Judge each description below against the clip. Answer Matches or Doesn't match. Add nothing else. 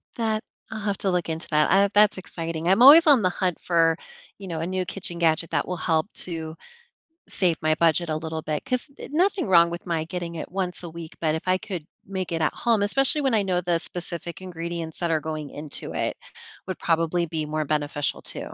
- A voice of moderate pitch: Matches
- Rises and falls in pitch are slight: Doesn't match